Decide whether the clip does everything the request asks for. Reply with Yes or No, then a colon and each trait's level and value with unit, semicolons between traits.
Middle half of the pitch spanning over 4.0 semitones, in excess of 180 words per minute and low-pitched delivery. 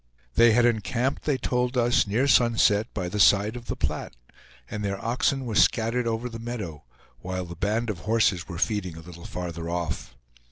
Yes: average, 4.6 semitones; average, 190 wpm; low, 110 Hz